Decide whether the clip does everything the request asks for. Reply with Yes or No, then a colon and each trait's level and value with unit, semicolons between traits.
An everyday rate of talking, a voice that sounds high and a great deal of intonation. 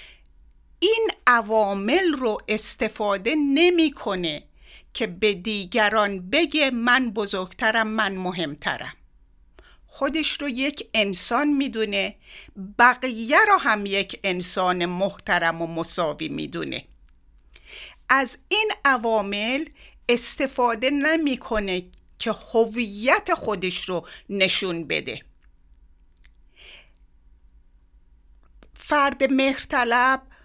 No: slow, 80 wpm; high, 215 Hz; wide, 7.2 semitones